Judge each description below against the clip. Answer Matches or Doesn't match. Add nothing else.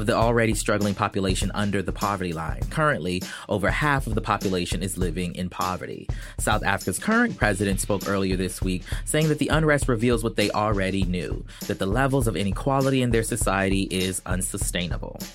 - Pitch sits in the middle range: Doesn't match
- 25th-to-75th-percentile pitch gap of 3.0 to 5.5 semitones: Matches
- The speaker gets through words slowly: Doesn't match